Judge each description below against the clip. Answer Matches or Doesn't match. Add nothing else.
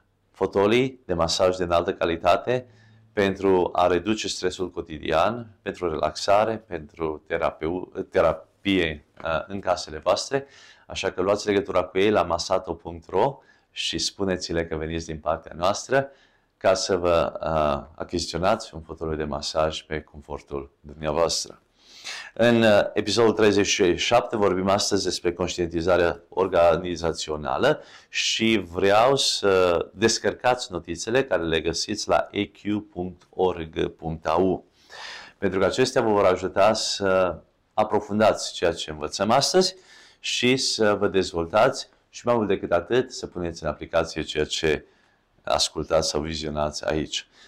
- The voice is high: Doesn't match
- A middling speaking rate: Doesn't match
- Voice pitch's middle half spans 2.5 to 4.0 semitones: Doesn't match